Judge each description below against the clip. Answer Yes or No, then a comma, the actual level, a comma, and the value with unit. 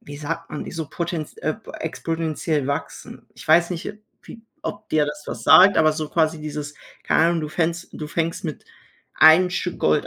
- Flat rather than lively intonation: Yes, narrow, 2.1 semitones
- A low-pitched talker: No, medium, 160 Hz